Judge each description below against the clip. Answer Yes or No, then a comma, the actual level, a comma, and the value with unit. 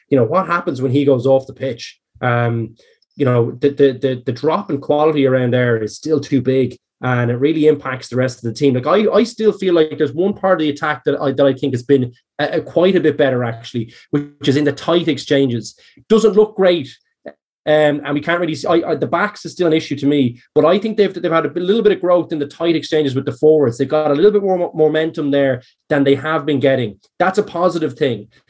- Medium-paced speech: No, fast, 255 wpm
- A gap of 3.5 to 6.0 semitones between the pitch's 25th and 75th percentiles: Yes, average, 4.2 semitones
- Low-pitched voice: No, medium, 145 Hz